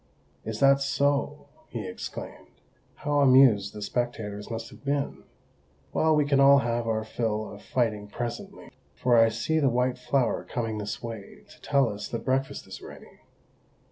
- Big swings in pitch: No, average, 4.0 semitones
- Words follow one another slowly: No, average, 165 wpm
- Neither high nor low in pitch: No, low, 120 Hz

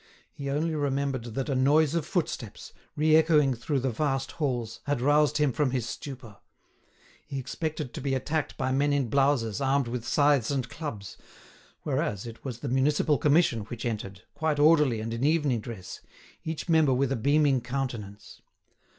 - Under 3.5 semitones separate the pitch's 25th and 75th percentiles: No, average, 3.8 semitones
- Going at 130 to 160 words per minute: No, average, 170 wpm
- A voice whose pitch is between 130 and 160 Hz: Yes, low, 135 Hz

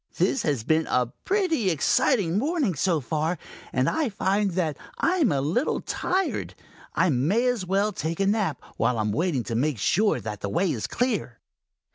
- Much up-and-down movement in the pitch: Yes, wide, 7.9 semitones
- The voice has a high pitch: No, medium, 180 Hz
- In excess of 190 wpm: No, average, 185 wpm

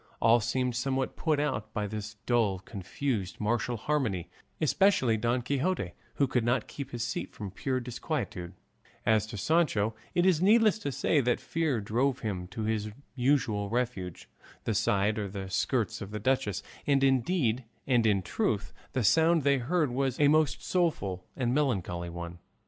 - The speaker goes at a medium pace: Yes, average, 165 wpm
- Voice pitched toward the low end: Yes, low, 120 Hz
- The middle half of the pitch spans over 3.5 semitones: Yes, average, 5.1 semitones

